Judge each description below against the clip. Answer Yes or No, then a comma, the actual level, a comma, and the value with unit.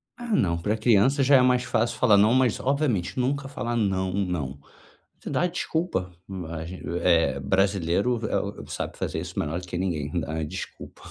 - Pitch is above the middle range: No, low, 100 Hz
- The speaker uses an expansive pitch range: Yes, wide, 6.5 semitones